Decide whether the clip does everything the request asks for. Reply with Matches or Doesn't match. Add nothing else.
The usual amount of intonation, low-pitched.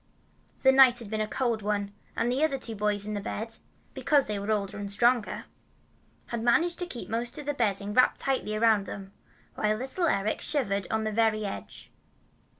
Doesn't match